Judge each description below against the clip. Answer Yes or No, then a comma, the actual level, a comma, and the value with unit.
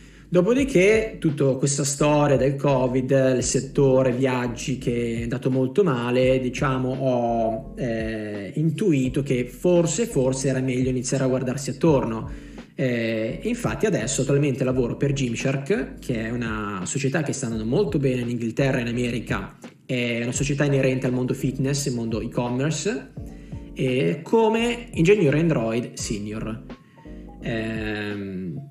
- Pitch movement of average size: Yes, average, 3.1 semitones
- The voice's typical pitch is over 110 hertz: Yes, low, 130 Hz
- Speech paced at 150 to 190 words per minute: No, average, 135 wpm